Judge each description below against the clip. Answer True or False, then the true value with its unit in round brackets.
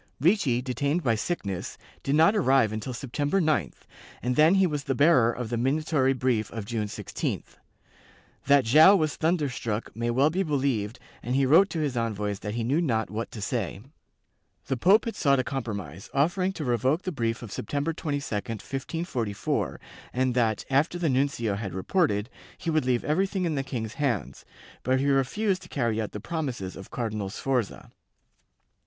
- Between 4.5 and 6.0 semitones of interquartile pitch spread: True (5.3 semitones)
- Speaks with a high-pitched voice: False (130 Hz)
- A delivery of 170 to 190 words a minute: True (175 wpm)